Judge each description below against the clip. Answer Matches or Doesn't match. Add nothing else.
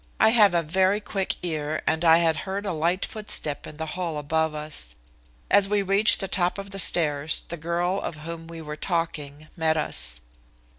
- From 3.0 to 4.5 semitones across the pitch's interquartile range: Matches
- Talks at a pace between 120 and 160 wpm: Doesn't match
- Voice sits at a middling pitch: Matches